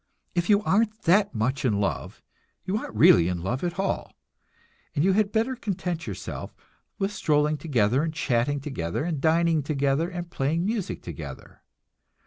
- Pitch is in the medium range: Yes, medium, 160 Hz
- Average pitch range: No, wide, 6.0 semitones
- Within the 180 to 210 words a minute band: No, average, 160 wpm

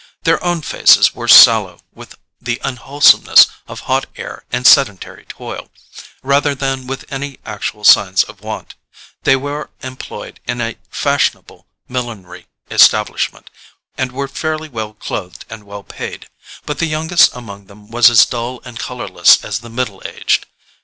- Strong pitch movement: No, average, 4.4 semitones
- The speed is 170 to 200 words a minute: No, average, 150 wpm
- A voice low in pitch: Yes, low, 125 Hz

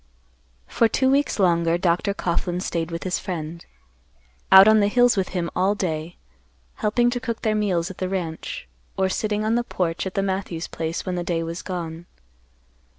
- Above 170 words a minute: Yes, average, 185 wpm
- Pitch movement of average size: Yes, average, 3.7 semitones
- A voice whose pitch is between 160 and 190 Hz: Yes, medium, 185 Hz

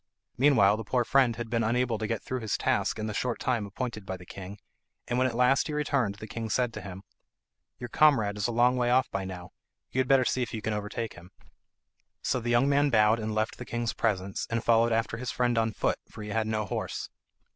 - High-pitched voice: No, low, 115 Hz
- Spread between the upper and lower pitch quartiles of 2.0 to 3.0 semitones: Yes, average, 2.7 semitones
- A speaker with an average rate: No, fast, 245 wpm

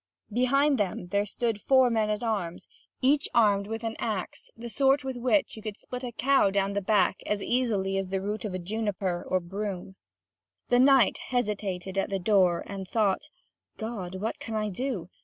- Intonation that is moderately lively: Yes, average, 3.8 semitones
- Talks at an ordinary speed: Yes, average, 185 wpm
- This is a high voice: Yes, high, 210 Hz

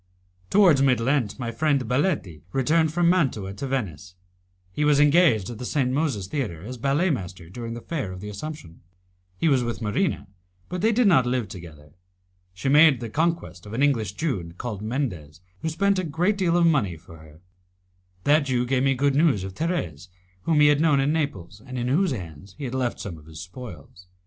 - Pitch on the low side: Yes, low, 130 Hz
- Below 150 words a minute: No, fast, 205 wpm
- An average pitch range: No, wide, 7.7 semitones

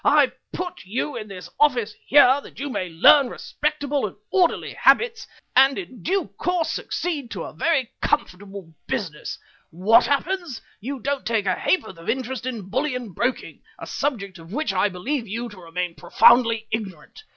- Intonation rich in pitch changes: Yes, wide, 6.6 semitones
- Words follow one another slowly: No, average, 165 wpm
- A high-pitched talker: Yes, high, 245 Hz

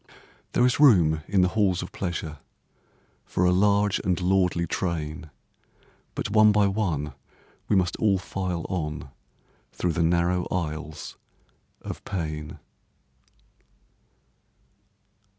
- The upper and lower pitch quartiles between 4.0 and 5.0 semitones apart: No, average, 3.3 semitones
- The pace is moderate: No, slow, 115 wpm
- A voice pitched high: No, very low, 90 Hz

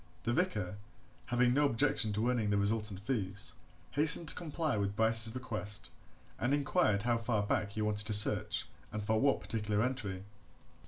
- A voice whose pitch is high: No, low, 110 Hz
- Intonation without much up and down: No, average, 3.4 semitones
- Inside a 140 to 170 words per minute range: Yes, average, 165 wpm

